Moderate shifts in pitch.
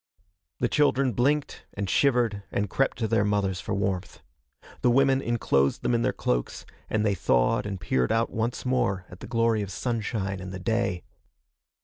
Yes: average, 4.0 semitones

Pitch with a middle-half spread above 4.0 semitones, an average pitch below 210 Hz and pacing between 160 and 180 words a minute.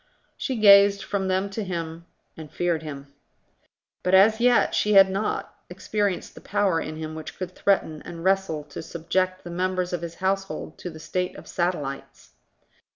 No: average, 3.2 semitones; medium, 185 Hz; average, 170 wpm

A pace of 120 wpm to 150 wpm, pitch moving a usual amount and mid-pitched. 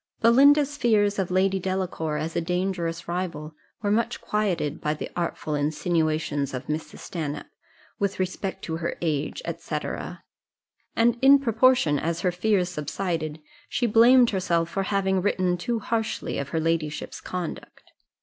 Yes: average, 145 wpm; average, 4.5 semitones; medium, 180 Hz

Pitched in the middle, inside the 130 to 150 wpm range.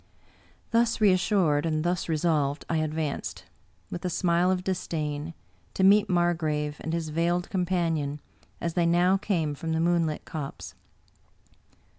Yes: medium, 170 Hz; average, 140 wpm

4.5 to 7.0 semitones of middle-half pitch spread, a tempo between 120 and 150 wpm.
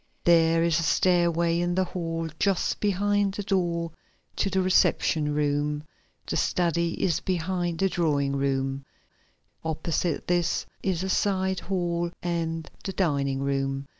No: average, 3.4 semitones; slow, 135 wpm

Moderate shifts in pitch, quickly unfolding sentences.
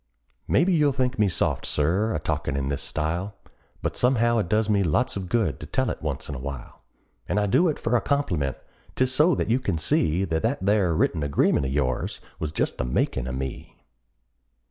No: wide, 8.2 semitones; fast, 210 wpm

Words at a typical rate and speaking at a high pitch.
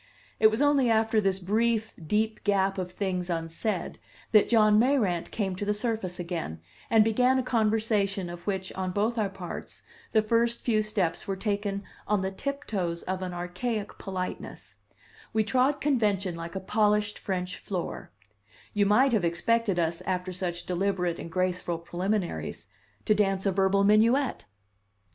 Yes: average, 160 wpm; high, 200 Hz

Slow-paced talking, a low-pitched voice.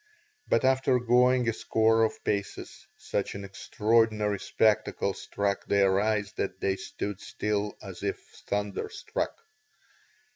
Yes: slow, 120 wpm; low, 105 Hz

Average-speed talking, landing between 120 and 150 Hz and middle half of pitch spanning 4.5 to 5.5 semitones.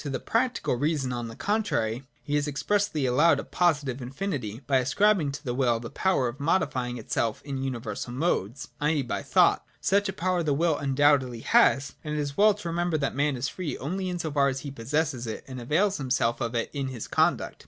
No: fast, 215 wpm; medium, 140 Hz; average, 4.8 semitones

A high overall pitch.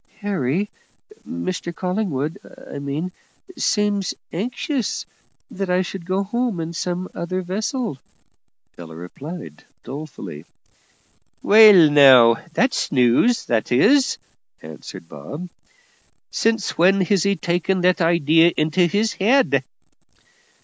No: medium, 180 Hz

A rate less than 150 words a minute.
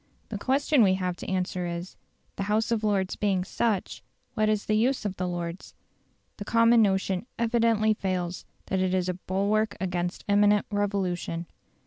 No: average, 165 wpm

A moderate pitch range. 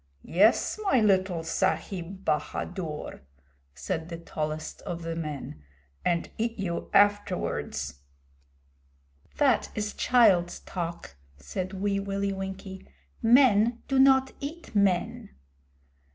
Yes: average, 4.1 semitones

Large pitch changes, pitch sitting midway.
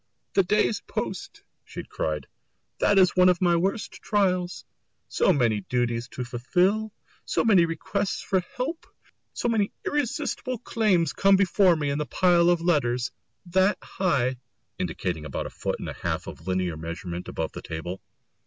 Yes: wide, 8.4 semitones; medium, 175 Hz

